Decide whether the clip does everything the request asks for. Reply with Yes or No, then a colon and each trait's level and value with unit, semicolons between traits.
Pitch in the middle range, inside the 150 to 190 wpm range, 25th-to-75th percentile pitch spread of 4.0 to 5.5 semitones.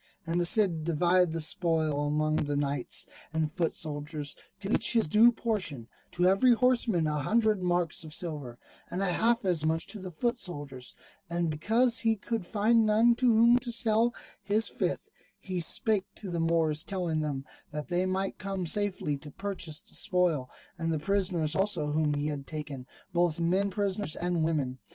Yes: medium, 175 Hz; average, 180 wpm; average, 5.0 semitones